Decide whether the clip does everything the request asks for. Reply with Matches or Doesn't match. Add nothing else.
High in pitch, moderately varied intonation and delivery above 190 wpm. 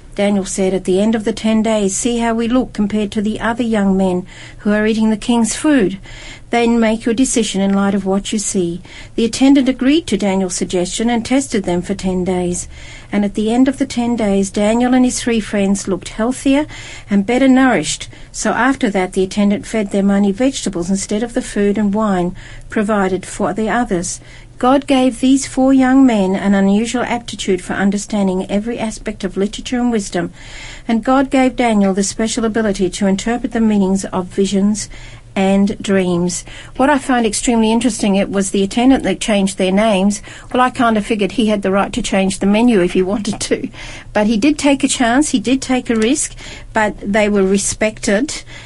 Matches